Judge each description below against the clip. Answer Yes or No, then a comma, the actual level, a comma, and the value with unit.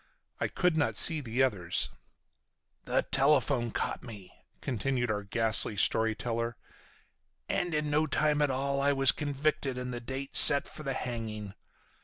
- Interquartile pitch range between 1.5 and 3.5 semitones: No, average, 4.0 semitones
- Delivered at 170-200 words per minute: No, average, 155 wpm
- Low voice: Yes, low, 130 Hz